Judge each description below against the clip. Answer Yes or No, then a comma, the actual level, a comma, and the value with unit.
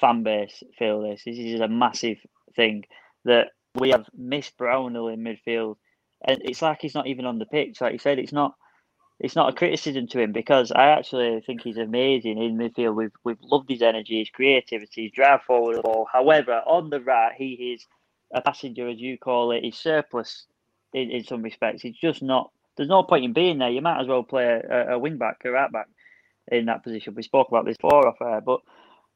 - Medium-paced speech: No, fast, 210 wpm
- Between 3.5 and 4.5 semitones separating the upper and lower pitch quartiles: No, average, 2.9 semitones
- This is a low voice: Yes, low, 125 Hz